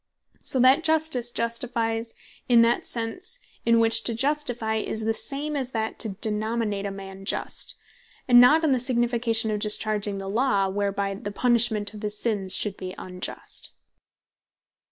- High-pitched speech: Yes, high, 225 Hz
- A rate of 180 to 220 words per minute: No, average, 155 wpm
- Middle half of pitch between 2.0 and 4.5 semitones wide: Yes, average, 3.0 semitones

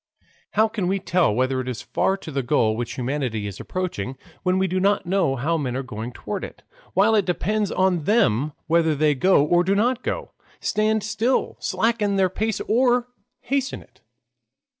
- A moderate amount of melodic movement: No, wide, 7.8 semitones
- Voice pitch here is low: No, medium, 185 Hz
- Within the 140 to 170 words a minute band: No, average, 185 wpm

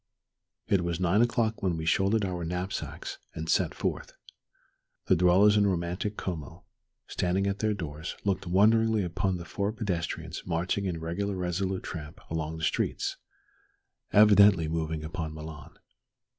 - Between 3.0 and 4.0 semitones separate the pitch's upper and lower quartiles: Yes, average, 3.6 semitones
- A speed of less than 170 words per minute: Yes, average, 145 wpm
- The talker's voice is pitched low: Yes, very low, 90 Hz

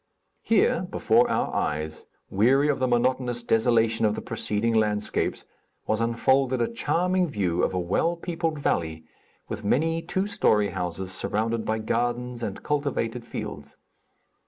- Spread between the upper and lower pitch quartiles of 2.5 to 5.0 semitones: Yes, average, 4.6 semitones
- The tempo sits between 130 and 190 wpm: Yes, average, 140 wpm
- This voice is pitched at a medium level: No, low, 115 Hz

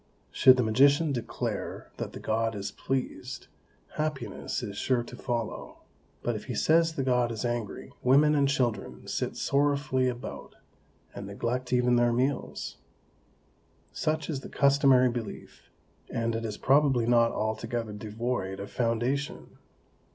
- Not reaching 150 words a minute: Yes, average, 140 wpm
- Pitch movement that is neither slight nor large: Yes, average, 3.2 semitones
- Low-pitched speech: Yes, low, 125 Hz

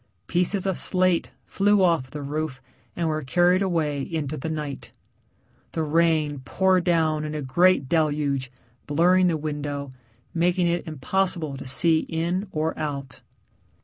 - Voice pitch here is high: No, medium, 160 Hz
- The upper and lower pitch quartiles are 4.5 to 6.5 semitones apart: No, average, 3.2 semitones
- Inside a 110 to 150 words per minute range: Yes, average, 145 wpm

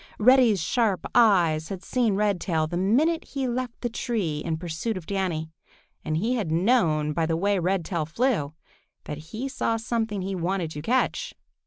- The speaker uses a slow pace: No, average, 170 wpm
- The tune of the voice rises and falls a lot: Yes, wide, 6.2 semitones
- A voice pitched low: No, high, 195 Hz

